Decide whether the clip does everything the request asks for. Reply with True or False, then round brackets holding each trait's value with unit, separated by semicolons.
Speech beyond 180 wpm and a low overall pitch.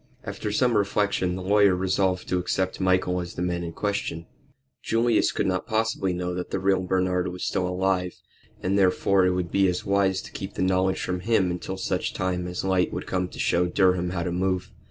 True (205 wpm; 95 Hz)